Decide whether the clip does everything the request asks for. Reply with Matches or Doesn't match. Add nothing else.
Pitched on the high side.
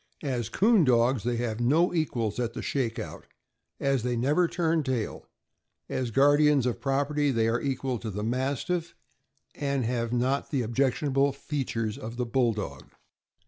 Doesn't match